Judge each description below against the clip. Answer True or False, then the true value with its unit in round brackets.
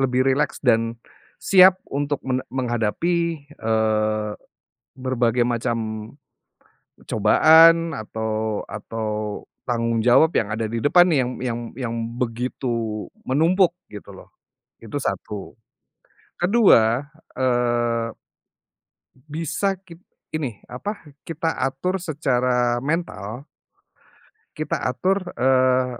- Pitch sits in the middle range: False (125 Hz)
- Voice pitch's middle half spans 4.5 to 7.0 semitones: True (5.5 semitones)